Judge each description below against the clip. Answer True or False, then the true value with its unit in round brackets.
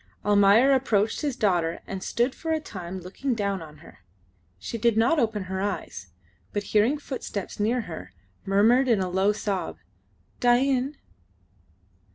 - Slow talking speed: False (150 wpm)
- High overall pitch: True (210 Hz)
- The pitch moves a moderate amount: True (4.6 semitones)